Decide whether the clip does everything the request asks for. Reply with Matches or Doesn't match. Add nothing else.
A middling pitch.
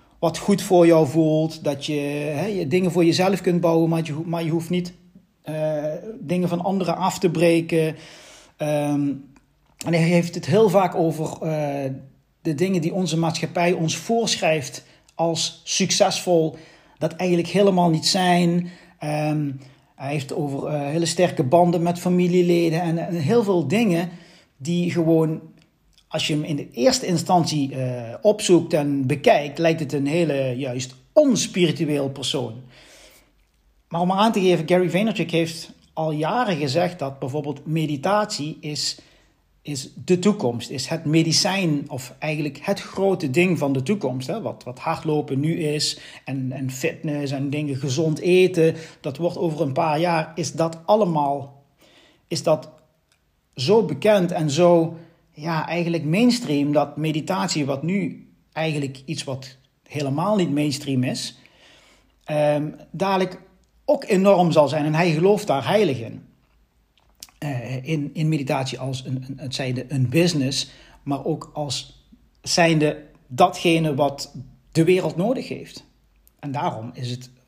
Matches